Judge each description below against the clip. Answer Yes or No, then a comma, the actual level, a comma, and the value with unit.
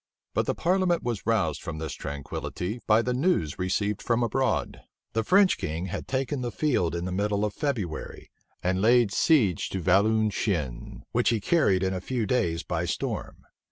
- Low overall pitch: Yes, low, 105 Hz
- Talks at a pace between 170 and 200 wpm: Yes, average, 175 wpm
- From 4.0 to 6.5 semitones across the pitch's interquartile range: Yes, wide, 5.6 semitones